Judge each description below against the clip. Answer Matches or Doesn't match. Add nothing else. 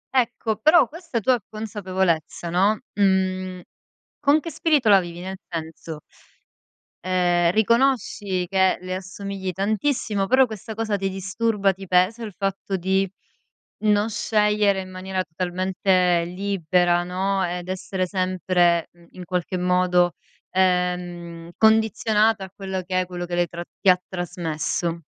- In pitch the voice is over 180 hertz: Matches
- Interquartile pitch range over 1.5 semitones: Matches